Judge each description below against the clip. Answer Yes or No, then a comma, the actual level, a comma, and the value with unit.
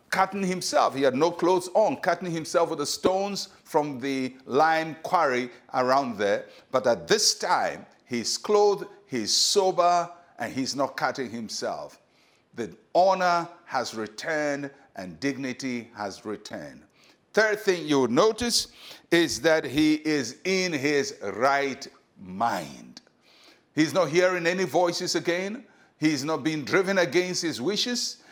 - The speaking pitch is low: No, medium, 165 Hz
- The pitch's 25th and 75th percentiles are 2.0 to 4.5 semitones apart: No, average, 5.1 semitones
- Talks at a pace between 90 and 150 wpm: Yes, average, 140 wpm